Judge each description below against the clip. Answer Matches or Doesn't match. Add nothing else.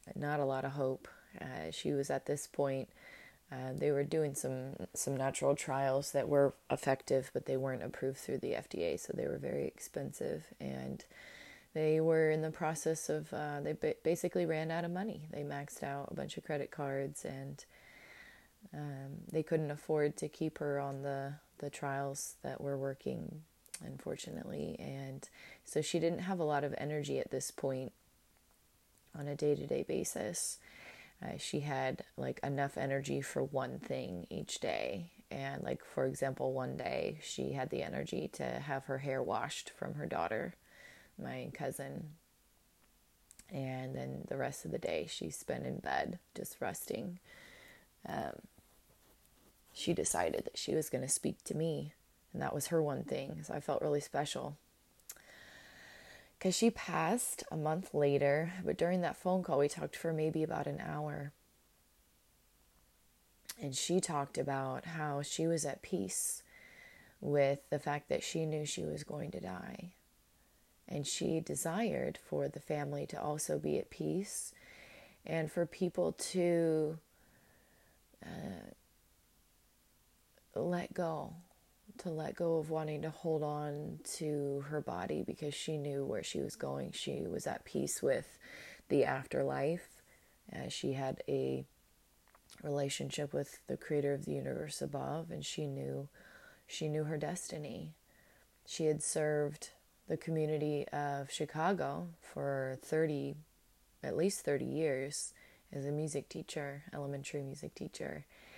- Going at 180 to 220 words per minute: Doesn't match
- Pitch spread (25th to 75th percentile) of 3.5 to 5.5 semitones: Doesn't match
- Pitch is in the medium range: Matches